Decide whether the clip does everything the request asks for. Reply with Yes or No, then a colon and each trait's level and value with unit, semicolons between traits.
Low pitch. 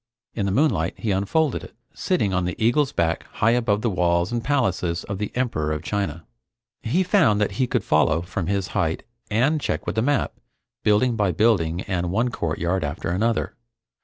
Yes: low, 100 Hz